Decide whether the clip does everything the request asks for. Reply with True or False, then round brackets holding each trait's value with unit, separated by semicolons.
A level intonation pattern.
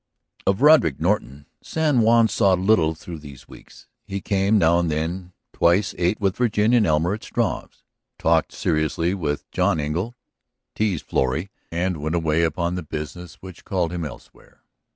False (4.0 semitones)